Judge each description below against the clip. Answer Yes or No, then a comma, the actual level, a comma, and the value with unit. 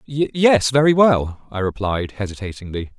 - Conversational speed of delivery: No, slow, 120 wpm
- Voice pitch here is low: Yes, low, 120 Hz